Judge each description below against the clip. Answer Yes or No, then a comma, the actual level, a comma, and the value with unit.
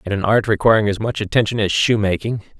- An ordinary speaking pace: No, fast, 210 wpm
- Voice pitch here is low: Yes, low, 105 Hz